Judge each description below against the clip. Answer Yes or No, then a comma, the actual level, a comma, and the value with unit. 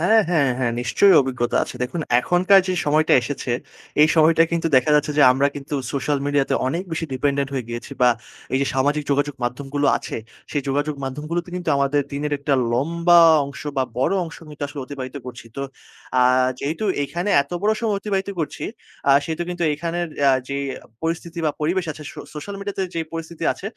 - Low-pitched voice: No, medium, 150 Hz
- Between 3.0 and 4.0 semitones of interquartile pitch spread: Yes, average, 3.5 semitones